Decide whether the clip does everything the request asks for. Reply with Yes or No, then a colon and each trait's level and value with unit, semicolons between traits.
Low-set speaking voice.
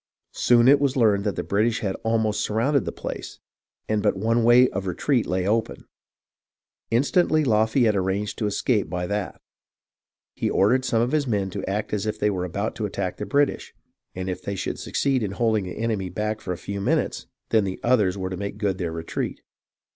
Yes: low, 105 Hz